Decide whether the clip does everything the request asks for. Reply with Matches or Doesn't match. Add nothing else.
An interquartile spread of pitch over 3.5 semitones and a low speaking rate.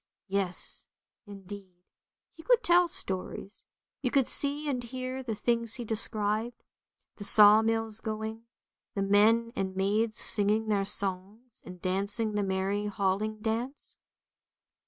Doesn't match